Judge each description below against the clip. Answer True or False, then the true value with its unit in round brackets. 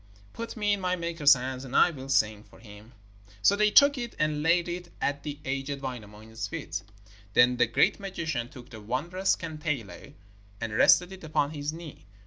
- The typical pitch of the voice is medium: True (145 Hz)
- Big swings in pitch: True (6.1 semitones)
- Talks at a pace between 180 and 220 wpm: True (185 wpm)